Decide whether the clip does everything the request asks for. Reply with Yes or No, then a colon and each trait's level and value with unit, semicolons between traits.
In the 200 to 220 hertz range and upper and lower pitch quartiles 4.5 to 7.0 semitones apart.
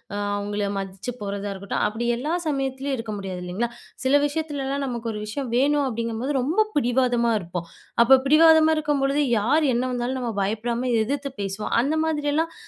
No: very high, 250 Hz; average, 5.0 semitones